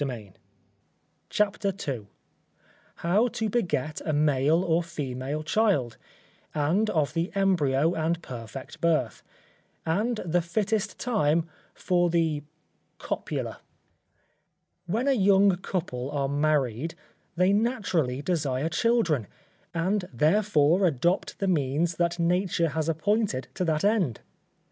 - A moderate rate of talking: No, slow, 110 wpm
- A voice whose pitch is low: No, medium, 170 Hz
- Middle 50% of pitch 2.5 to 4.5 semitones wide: No, average, 5.0 semitones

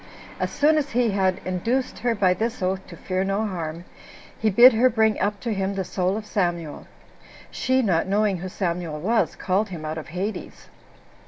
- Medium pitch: No, high, 195 Hz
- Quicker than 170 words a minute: Yes, average, 190 wpm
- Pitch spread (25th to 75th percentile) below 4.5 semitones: Yes, average, 3.5 semitones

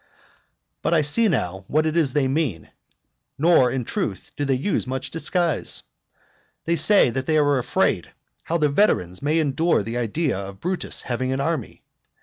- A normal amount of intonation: Yes, average, 4.6 semitones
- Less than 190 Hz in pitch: Yes, medium, 140 Hz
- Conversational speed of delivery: Yes, average, 170 wpm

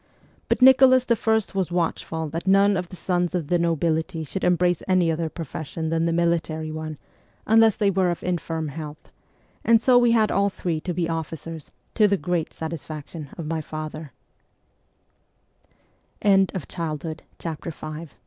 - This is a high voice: No, medium, 170 Hz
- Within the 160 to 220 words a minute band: No, slow, 135 wpm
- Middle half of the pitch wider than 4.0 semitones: No, average, 3.3 semitones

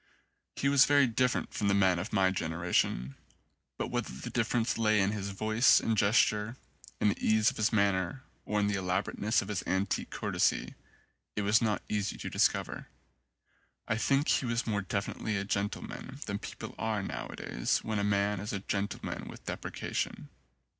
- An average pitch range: No, narrow, 2.1 semitones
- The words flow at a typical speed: Yes, average, 175 wpm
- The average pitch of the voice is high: No, low, 105 Hz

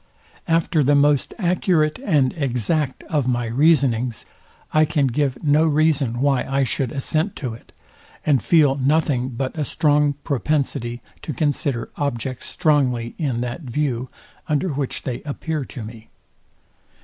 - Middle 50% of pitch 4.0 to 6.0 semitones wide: No, average, 3.5 semitones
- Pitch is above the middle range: No, medium, 140 Hz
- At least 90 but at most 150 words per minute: Yes, average, 140 wpm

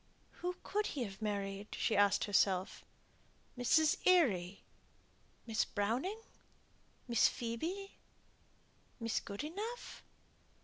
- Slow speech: Yes, slow, 90 wpm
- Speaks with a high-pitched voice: Yes, high, 230 Hz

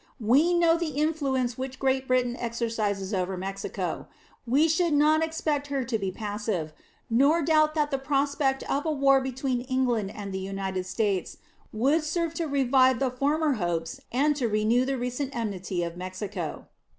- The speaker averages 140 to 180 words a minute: Yes, average, 165 wpm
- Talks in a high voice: Yes, very high, 255 Hz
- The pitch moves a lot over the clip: Yes, wide, 5.7 semitones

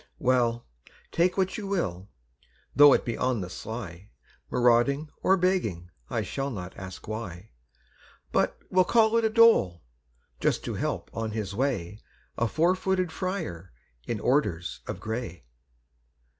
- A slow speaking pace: No, average, 145 wpm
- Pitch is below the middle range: Yes, low, 120 Hz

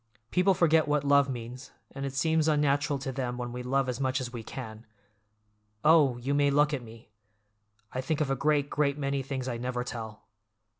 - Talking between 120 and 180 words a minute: No, average, 200 wpm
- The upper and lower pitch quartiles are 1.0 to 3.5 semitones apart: Yes, average, 2.8 semitones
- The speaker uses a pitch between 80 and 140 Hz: Yes, low, 135 Hz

